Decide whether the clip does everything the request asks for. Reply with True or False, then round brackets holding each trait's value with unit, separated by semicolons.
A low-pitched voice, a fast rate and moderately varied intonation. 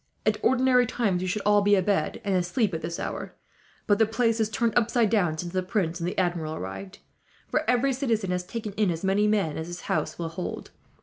False (200 Hz; 225 wpm; 4.2 semitones)